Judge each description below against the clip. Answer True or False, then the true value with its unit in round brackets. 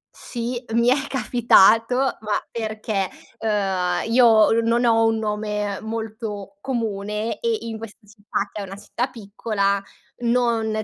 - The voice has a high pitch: True (220 Hz)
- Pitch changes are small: True (2.2 semitones)